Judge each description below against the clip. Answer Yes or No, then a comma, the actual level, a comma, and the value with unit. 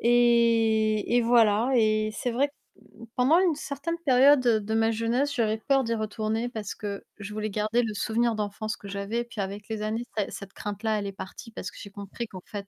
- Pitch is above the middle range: Yes, high, 220 Hz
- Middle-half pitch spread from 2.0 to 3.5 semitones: Yes, narrow, 2.4 semitones